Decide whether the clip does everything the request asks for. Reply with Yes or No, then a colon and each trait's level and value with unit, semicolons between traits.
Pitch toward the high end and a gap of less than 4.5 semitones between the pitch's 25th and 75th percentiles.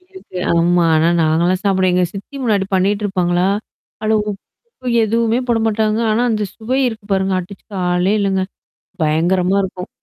Yes: high, 195 Hz; average, 3.4 semitones